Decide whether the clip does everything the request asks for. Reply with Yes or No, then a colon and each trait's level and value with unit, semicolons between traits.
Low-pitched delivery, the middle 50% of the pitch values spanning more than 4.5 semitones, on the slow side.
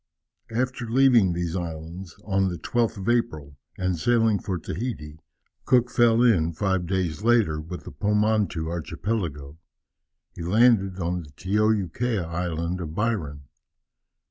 Yes: very low, 95 Hz; average, 5.2 semitones; slow, 130 wpm